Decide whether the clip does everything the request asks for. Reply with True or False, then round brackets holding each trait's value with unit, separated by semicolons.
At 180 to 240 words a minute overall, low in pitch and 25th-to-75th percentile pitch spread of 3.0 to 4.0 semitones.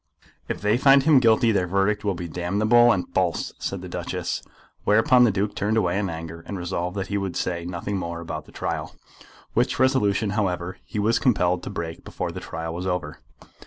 True (200 wpm; 95 Hz; 3.6 semitones)